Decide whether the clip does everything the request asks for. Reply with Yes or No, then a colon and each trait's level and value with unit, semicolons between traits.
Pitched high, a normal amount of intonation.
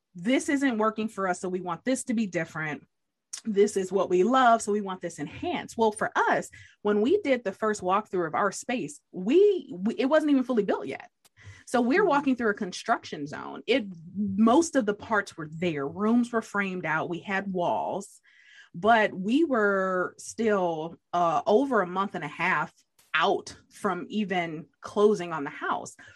Yes: high, 205 Hz; average, 4.4 semitones